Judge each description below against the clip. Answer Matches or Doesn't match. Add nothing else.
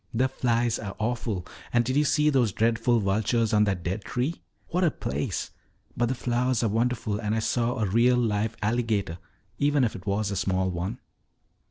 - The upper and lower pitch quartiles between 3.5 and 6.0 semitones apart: Doesn't match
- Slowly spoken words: Doesn't match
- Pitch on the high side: Doesn't match